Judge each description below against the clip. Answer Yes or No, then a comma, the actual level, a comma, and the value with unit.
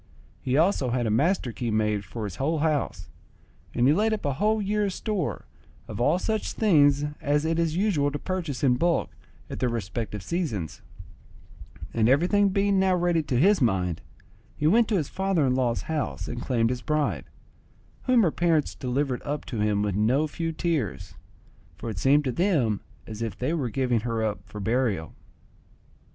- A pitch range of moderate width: No, wide, 6.7 semitones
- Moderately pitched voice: Yes, medium, 145 Hz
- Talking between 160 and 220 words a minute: Yes, average, 185 wpm